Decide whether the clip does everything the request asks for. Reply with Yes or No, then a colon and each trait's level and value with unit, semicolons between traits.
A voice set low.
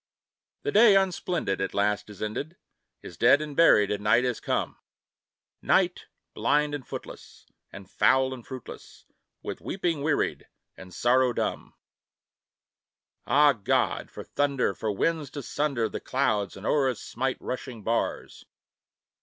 Yes: low, 130 Hz